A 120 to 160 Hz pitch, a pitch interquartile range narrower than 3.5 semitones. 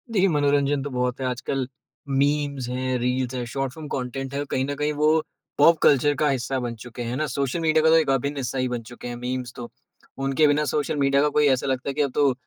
Yes: low, 135 Hz; narrow, 2.6 semitones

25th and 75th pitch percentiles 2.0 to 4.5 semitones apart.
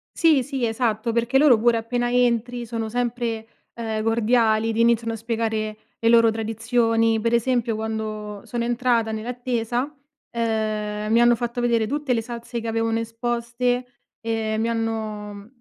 No: narrow, 1.4 semitones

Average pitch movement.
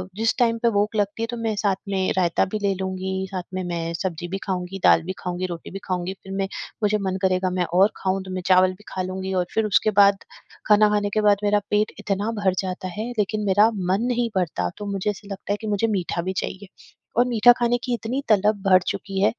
No: narrow, 2.2 semitones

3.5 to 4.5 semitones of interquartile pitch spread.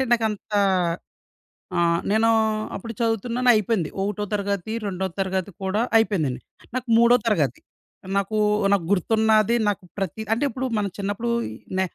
No: average, 2.9 semitones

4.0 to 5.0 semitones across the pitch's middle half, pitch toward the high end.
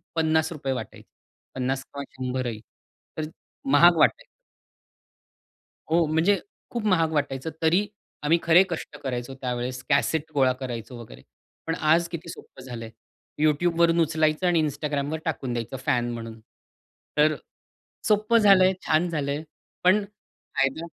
No: average, 4.4 semitones; medium, 155 Hz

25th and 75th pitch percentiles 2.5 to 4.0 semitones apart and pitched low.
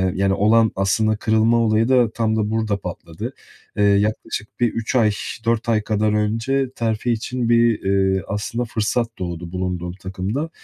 Yes: average, 2.9 semitones; low, 110 Hz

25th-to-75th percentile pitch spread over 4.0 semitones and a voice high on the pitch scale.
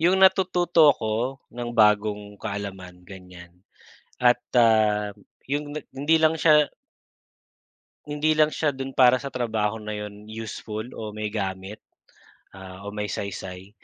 No: average, 5.2 semitones; low, 110 Hz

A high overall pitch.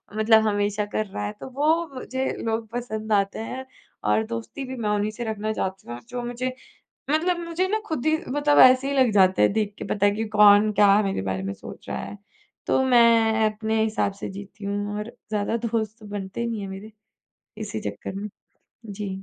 Yes: high, 215 Hz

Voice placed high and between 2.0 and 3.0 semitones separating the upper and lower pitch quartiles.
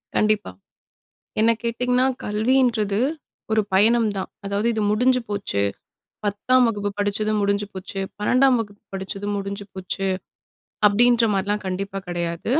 Yes: high, 205 Hz; narrow, 2.5 semitones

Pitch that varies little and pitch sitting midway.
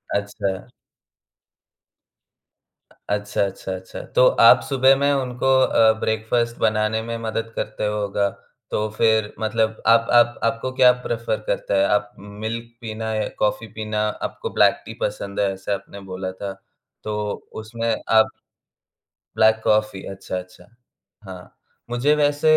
No: narrow, 2.2 semitones; low, 110 Hz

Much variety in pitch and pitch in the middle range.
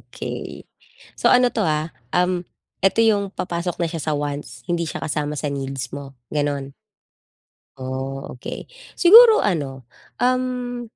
Yes: wide, 6.6 semitones; medium, 160 Hz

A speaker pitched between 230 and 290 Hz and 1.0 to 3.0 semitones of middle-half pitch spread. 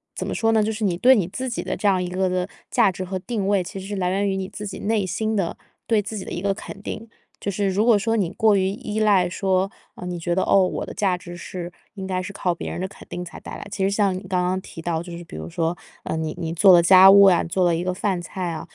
No: high, 190 Hz; narrow, 2.4 semitones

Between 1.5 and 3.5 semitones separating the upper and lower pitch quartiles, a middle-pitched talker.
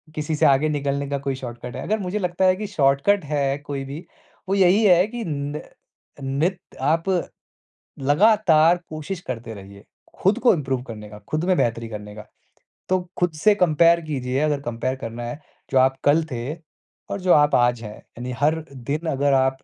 No: average, 5.1 semitones; medium, 145 Hz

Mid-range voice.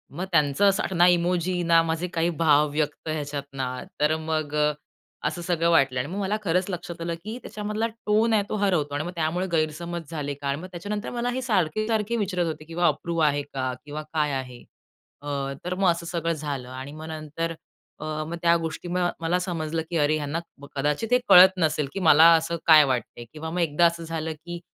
Yes: medium, 165 Hz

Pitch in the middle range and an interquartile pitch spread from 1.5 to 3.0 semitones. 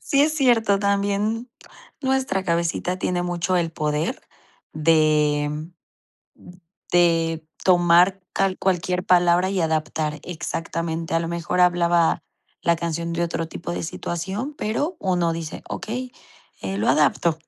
Yes: medium, 175 Hz; average, 2.7 semitones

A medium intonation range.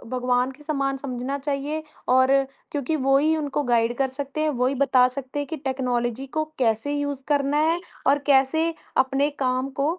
No: narrow, 2.1 semitones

